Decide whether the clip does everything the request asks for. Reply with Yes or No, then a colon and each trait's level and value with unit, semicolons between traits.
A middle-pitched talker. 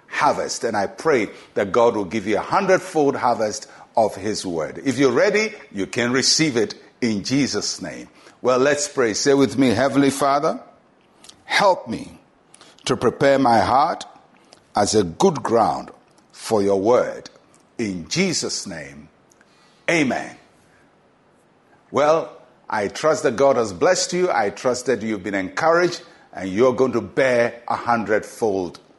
No: low, 130 Hz